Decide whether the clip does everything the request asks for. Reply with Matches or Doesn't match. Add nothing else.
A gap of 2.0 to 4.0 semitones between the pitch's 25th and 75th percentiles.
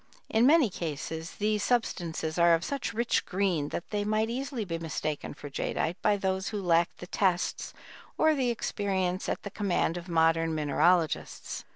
Doesn't match